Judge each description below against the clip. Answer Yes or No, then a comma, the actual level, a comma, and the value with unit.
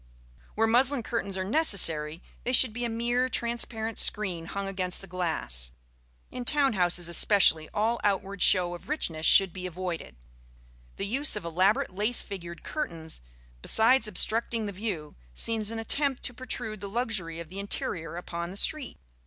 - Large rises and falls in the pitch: No, average, 4.9 semitones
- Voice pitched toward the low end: No, high, 200 Hz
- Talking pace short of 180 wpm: Yes, average, 160 wpm